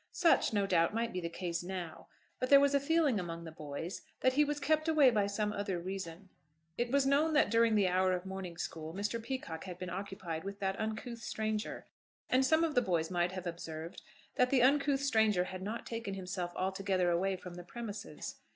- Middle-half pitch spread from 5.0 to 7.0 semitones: Yes, wide, 5.6 semitones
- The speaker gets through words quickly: Yes, fast, 210 wpm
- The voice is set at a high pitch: Yes, high, 200 Hz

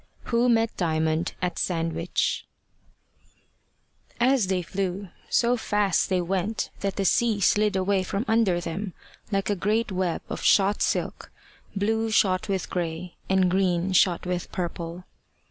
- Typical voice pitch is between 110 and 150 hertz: No, high, 190 Hz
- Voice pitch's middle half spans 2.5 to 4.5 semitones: Yes, average, 2.8 semitones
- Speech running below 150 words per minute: Yes, average, 140 wpm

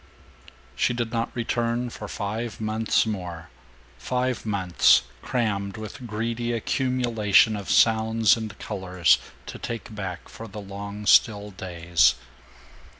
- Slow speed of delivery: Yes, slow, 120 wpm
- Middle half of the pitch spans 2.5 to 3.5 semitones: Yes, average, 2.8 semitones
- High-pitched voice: No, low, 110 Hz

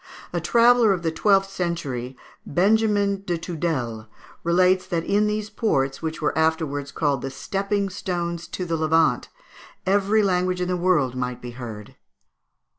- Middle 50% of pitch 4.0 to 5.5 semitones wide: Yes, average, 5.1 semitones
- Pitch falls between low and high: Yes, medium, 175 Hz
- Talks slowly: No, average, 150 wpm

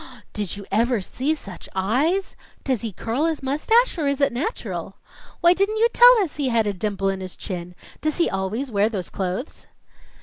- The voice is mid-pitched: No, high, 245 Hz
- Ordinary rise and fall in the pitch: No, wide, 8.0 semitones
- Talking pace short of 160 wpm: No, average, 195 wpm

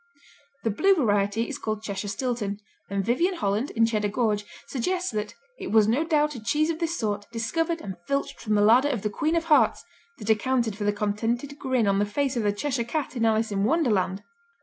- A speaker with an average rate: No, fast, 215 wpm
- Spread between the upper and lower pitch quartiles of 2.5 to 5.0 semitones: No, wide, 5.5 semitones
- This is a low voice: No, high, 225 Hz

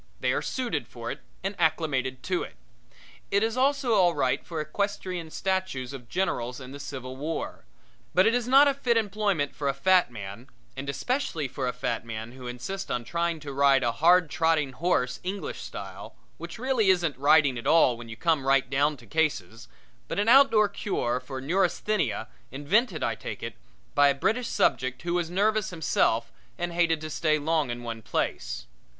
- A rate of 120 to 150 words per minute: No, average, 190 wpm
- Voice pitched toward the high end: No, medium, 155 Hz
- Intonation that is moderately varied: No, wide, 6.6 semitones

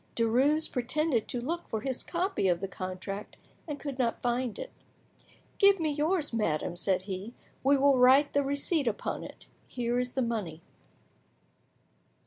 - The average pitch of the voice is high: Yes, very high, 250 Hz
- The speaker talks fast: No, average, 155 wpm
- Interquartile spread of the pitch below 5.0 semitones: No, average, 5.3 semitones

